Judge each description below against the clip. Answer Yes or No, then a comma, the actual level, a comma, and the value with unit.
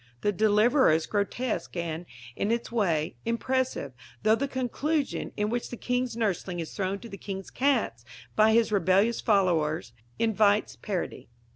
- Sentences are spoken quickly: No, average, 150 wpm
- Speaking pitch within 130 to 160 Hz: No, high, 215 Hz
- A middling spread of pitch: Yes, average, 4.3 semitones